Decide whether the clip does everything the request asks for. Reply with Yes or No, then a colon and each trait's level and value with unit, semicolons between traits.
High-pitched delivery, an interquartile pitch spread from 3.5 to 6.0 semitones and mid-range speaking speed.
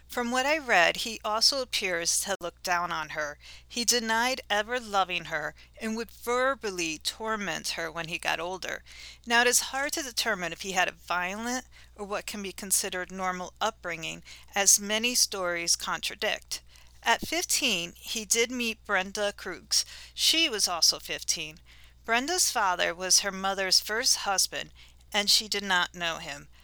Yes: high, 200 Hz; average, 5.1 semitones; average, 160 wpm